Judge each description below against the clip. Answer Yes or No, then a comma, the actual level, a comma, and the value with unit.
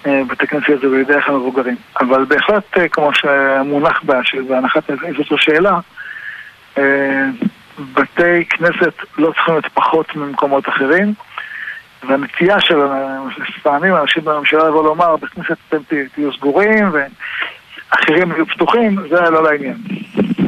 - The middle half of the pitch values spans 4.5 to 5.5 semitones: No, average, 4.0 semitones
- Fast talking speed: No, average, 115 wpm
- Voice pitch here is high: No, medium, 150 Hz